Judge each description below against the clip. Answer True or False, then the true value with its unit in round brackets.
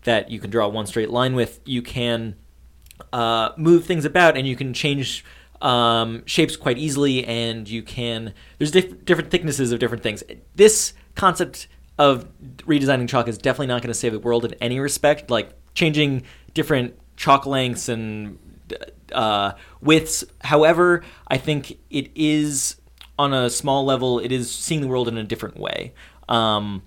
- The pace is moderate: True (170 wpm)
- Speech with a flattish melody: False (4.3 semitones)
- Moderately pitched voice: False (125 Hz)